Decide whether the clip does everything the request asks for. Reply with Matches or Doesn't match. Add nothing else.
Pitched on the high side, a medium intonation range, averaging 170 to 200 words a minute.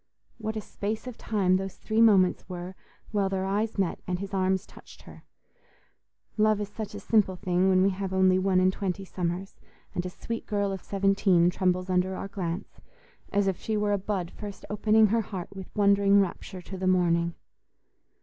Doesn't match